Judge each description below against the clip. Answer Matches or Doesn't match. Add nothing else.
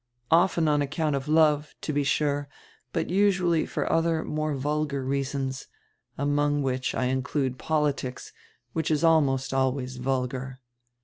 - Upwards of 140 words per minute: Doesn't match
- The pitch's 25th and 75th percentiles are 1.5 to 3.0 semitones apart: Matches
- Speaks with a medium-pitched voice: Matches